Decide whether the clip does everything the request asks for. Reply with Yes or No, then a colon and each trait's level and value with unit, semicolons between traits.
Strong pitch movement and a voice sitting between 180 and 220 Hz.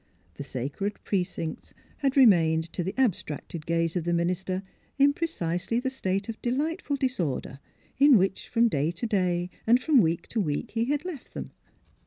Yes: wide, 7.3 semitones; high, 190 Hz